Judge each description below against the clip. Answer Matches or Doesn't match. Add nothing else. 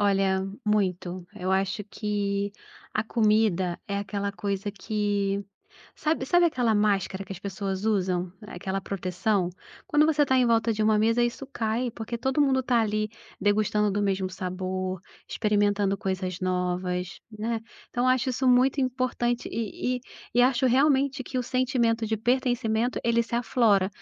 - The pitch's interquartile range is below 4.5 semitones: Matches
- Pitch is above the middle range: Matches